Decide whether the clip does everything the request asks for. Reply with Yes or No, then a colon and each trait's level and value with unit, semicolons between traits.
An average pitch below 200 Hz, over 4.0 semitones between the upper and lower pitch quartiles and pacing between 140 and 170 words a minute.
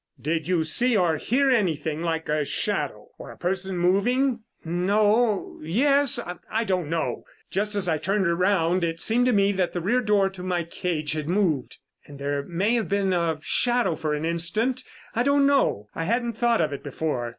No: medium, 185 Hz; wide, 5.6 semitones; average, 190 wpm